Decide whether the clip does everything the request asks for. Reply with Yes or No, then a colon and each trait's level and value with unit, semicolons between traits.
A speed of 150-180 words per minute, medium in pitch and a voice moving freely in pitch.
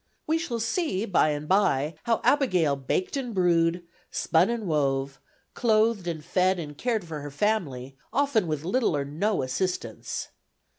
Yes: average, 155 wpm; medium, 180 Hz; wide, 7.0 semitones